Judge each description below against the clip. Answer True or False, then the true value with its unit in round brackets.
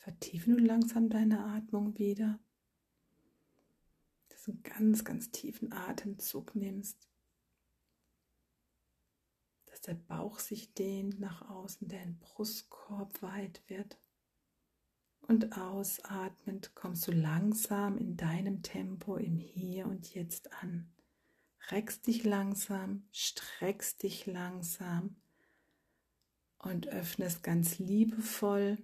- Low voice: False (195 Hz)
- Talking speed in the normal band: False (100 wpm)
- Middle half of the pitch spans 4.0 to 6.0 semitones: False (2.9 semitones)